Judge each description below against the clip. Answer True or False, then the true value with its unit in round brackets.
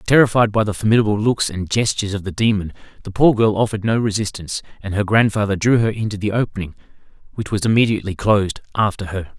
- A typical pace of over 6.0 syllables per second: True (6.7 syllables/s)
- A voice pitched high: False (105 Hz)